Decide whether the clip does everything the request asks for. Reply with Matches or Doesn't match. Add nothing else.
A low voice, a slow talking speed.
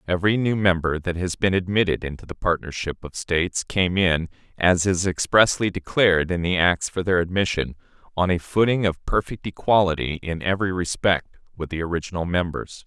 Doesn't match